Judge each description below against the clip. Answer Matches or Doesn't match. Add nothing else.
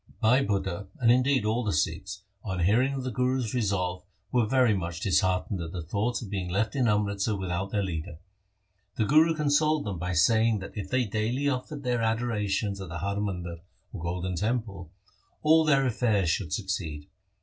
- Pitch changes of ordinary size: Matches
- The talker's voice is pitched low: Matches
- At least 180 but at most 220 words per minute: Matches